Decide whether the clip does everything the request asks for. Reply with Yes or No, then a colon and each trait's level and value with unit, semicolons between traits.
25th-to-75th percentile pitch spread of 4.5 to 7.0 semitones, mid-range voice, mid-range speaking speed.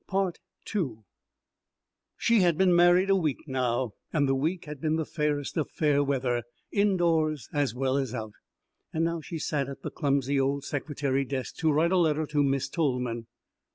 No: average, 3.3 semitones; medium, 145 Hz; average, 165 wpm